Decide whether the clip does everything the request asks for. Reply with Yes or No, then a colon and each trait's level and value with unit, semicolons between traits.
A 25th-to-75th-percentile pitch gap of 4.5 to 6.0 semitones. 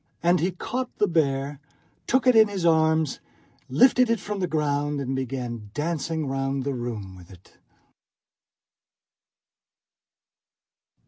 Yes: average, 5.0 semitones